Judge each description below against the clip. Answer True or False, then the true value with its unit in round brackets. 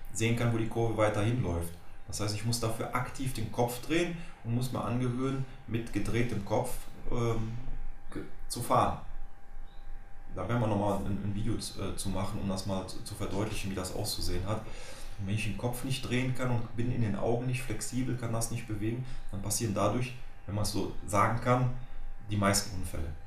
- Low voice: True (110 Hz)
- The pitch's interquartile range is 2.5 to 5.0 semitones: True (3.3 semitones)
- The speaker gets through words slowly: False (190 wpm)